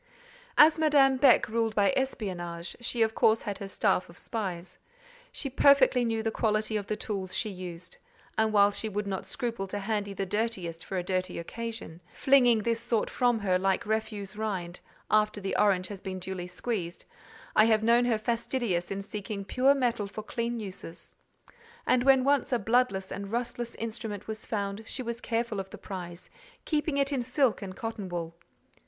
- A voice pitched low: No, high, 215 Hz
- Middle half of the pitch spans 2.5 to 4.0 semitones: Yes, average, 3.5 semitones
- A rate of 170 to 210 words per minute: Yes, average, 180 wpm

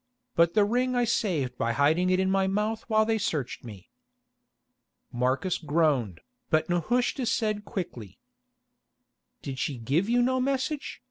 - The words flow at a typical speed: Yes, average, 145 wpm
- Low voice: No, medium, 185 Hz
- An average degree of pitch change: No, wide, 8.0 semitones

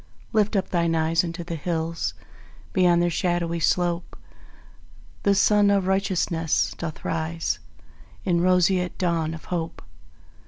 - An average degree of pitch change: No, narrow, 1.9 semitones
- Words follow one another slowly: Yes, slow, 125 wpm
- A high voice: No, medium, 175 Hz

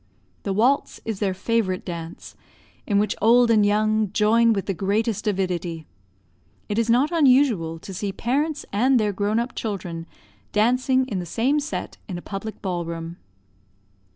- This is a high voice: Yes, high, 210 Hz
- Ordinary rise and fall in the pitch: Yes, average, 4.0 semitones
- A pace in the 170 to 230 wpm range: No, average, 160 wpm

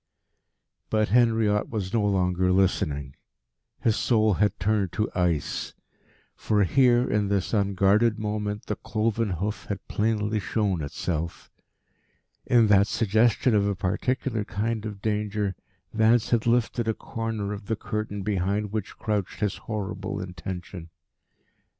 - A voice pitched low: Yes, low, 105 Hz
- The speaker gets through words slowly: Yes, slow, 130 wpm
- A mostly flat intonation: Yes, narrow, 2.2 semitones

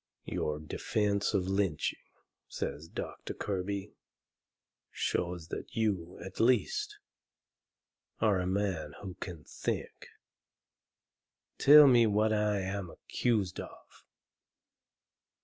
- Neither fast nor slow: No, slow, 95 wpm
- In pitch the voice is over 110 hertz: No, low, 100 Hz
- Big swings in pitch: No, average, 2.9 semitones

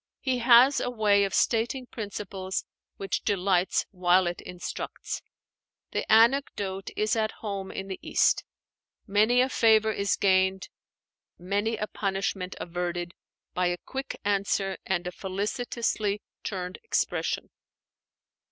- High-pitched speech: Yes, high, 200 Hz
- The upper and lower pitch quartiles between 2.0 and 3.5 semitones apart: Yes, average, 2.9 semitones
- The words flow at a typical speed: No, slow, 125 wpm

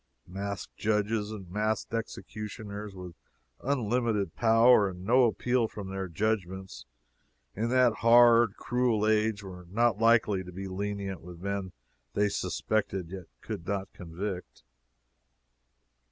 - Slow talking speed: Yes, slow, 125 wpm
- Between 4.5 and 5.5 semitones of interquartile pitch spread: No, average, 3.0 semitones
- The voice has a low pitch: Yes, low, 105 Hz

